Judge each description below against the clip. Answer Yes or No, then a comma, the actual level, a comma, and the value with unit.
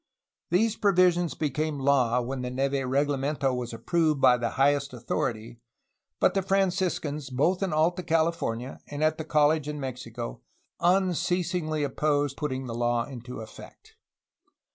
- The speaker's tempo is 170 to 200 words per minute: No, average, 140 wpm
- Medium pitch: Yes, medium, 145 Hz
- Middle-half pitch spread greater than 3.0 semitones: Yes, average, 4.6 semitones